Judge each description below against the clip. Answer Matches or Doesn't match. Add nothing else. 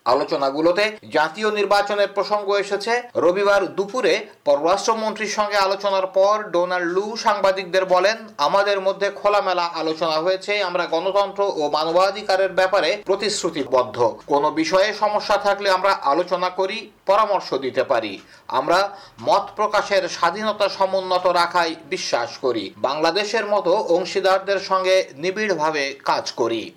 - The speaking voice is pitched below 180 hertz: Doesn't match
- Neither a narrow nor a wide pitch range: Doesn't match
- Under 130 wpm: Matches